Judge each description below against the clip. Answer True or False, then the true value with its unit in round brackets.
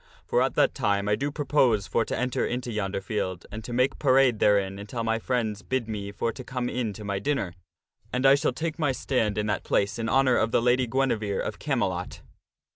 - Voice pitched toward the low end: True (115 Hz)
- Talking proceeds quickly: True (220 wpm)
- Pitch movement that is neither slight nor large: True (3.7 semitones)